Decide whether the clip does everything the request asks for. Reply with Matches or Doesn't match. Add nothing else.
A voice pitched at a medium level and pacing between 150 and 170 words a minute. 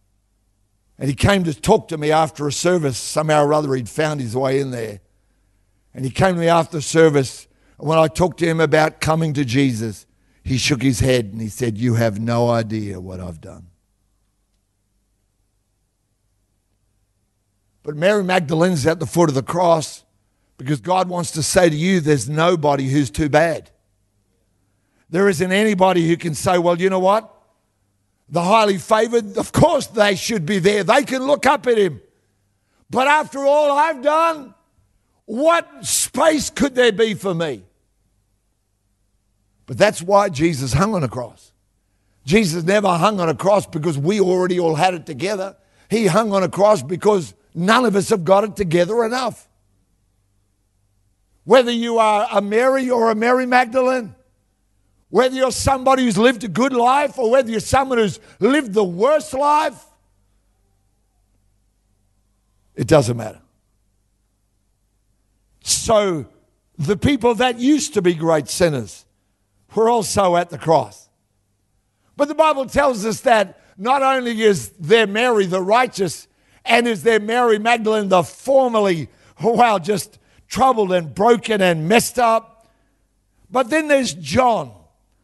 Matches